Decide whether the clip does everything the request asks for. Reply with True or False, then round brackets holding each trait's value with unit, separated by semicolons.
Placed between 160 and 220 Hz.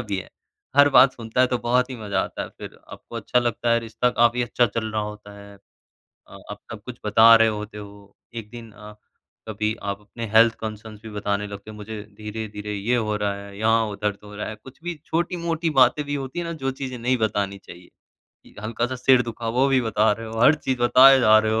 False (110 Hz)